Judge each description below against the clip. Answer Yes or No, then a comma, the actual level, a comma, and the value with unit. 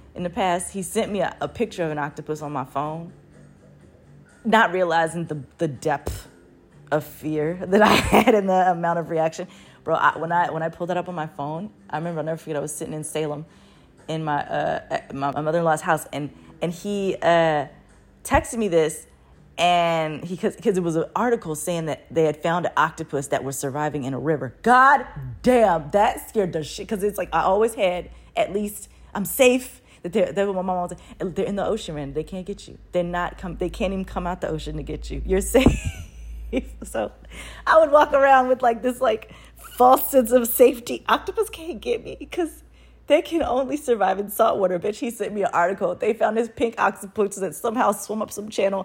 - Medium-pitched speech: Yes, medium, 180 Hz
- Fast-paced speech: Yes, fast, 215 wpm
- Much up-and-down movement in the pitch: Yes, wide, 5.7 semitones